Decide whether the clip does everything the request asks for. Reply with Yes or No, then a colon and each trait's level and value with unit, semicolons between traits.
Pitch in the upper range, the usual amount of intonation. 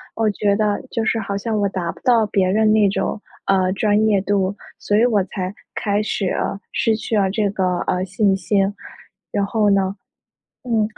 No: high, 205 Hz; narrow, 1.9 semitones